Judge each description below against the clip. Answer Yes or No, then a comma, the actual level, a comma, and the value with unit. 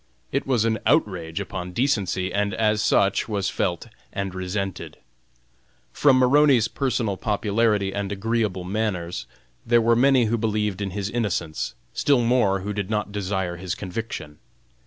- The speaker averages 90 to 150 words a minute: Yes, average, 145 wpm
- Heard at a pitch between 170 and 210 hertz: No, low, 105 Hz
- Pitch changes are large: No, average, 3.3 semitones